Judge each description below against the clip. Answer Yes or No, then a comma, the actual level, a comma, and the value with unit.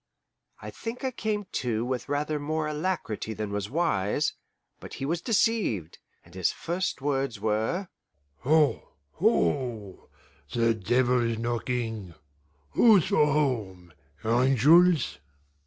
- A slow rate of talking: Yes, slow, 115 wpm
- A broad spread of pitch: Yes, wide, 6.3 semitones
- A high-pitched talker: No, low, 130 Hz